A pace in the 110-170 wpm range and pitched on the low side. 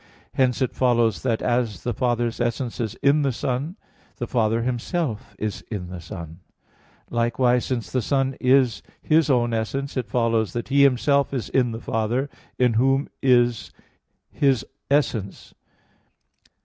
Yes: average, 150 wpm; low, 120 Hz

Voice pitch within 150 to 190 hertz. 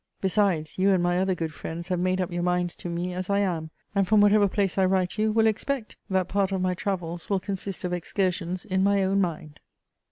Yes: medium, 185 Hz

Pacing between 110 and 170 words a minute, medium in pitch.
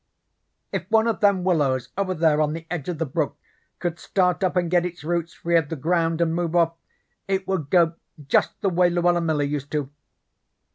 No: fast, 205 wpm; medium, 170 Hz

